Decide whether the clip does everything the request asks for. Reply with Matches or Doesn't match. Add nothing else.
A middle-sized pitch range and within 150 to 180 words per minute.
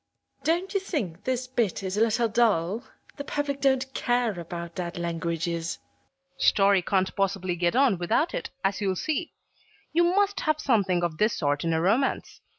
Doesn't match